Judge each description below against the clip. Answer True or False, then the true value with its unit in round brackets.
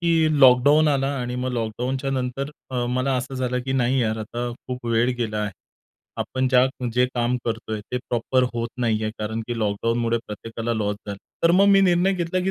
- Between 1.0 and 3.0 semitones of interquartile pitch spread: True (2.7 semitones)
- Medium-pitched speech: False (125 Hz)